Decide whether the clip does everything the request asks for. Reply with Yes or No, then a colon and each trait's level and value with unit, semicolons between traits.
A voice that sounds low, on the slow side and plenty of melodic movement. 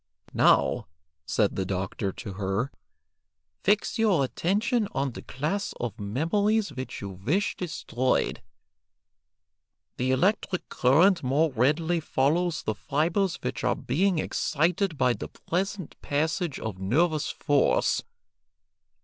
No: medium, 155 Hz; slow, 115 wpm; wide, 6.5 semitones